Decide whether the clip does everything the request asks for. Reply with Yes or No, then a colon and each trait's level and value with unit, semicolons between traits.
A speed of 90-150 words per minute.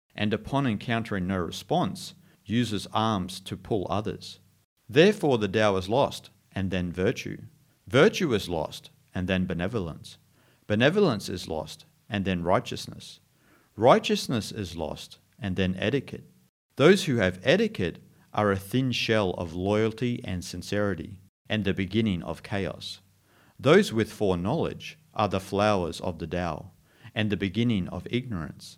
Yes: average, 140 wpm